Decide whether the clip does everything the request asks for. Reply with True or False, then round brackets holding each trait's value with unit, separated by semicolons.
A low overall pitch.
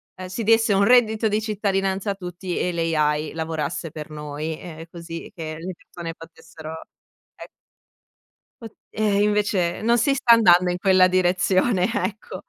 False (185 Hz)